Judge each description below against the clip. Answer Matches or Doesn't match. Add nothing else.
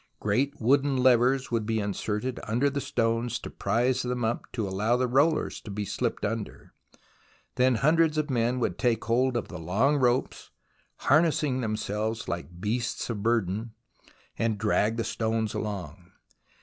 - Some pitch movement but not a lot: Matches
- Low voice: Matches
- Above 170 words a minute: Doesn't match